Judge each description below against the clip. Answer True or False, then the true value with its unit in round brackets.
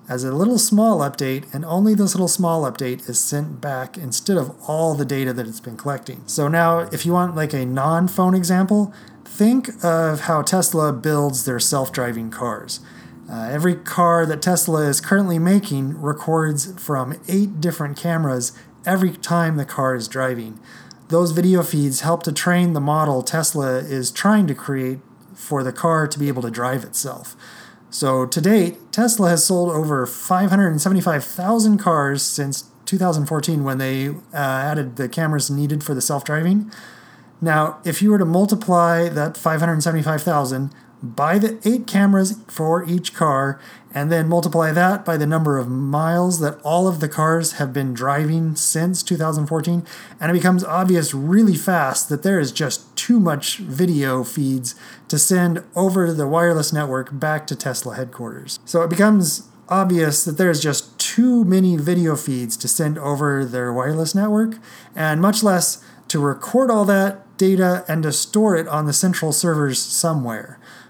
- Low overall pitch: False (160 Hz)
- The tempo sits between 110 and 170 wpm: True (165 wpm)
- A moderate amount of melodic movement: True (4.3 semitones)